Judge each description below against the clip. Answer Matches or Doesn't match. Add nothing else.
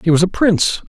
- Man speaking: Matches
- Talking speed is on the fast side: Matches